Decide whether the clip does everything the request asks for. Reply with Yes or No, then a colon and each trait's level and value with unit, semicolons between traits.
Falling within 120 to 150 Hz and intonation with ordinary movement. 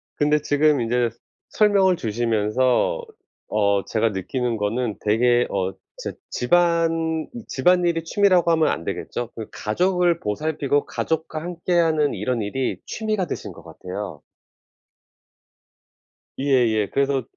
No: medium, 140 Hz; wide, 6.7 semitones